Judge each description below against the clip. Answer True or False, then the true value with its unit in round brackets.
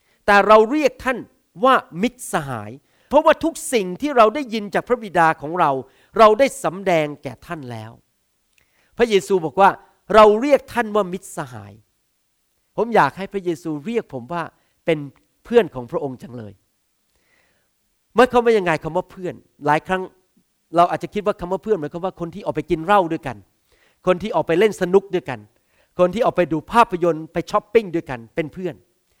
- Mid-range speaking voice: True (180 Hz)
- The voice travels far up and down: True (6.0 semitones)